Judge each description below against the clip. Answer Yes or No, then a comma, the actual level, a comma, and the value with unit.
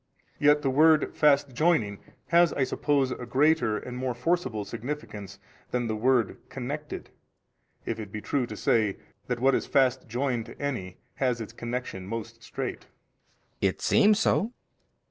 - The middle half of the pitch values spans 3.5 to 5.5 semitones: Yes, average, 4.4 semitones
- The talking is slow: No, average, 160 wpm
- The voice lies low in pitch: Yes, low, 130 Hz